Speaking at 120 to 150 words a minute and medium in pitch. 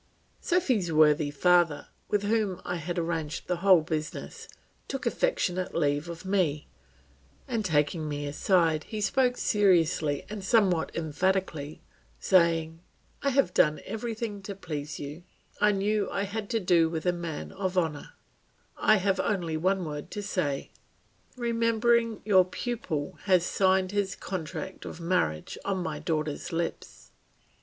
Yes: average, 140 wpm; medium, 180 Hz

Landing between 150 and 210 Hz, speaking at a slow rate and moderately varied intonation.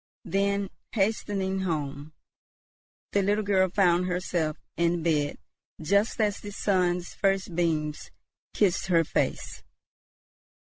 Yes: medium, 185 Hz; slow, 105 wpm; average, 3.0 semitones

